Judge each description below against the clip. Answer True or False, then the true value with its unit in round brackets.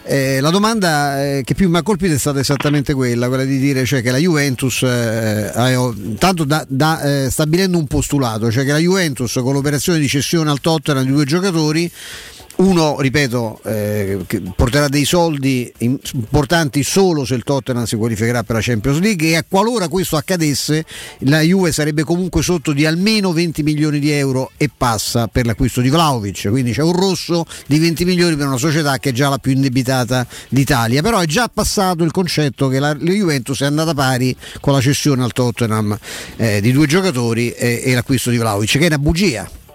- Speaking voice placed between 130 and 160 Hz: True (140 Hz)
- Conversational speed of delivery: False (190 wpm)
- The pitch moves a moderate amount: True (4.3 semitones)